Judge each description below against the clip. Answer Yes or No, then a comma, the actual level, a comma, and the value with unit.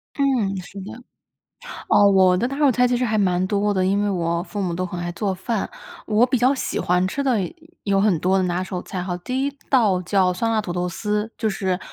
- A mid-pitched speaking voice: No, high, 195 Hz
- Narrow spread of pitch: No, average, 3.8 semitones